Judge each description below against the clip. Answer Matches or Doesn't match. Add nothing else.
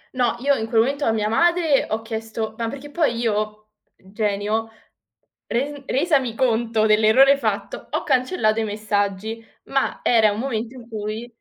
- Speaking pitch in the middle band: Doesn't match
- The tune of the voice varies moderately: Matches